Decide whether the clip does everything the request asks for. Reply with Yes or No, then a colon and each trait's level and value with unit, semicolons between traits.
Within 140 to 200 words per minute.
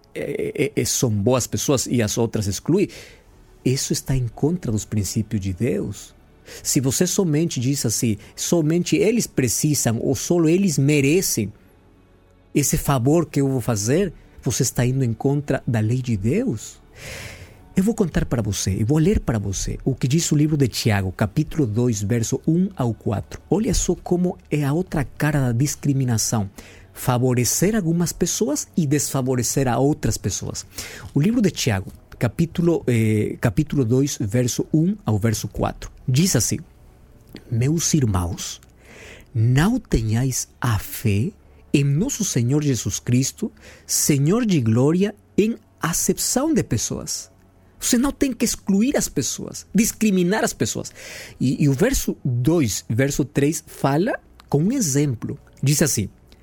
Yes: average, 150 wpm